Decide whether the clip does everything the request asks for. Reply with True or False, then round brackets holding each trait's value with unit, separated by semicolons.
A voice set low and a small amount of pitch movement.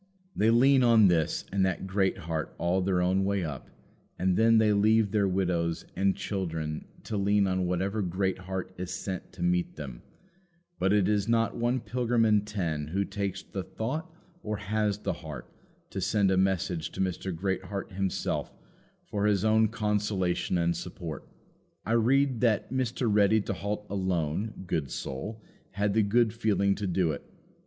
False (100 Hz; 3.0 semitones)